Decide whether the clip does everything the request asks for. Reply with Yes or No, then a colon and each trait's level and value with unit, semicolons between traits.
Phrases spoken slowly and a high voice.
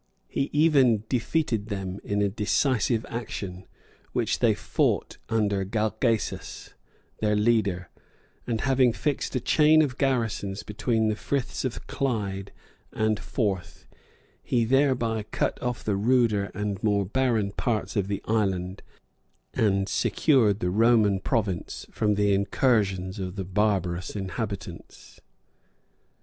No: slow, 125 wpm; low, 105 Hz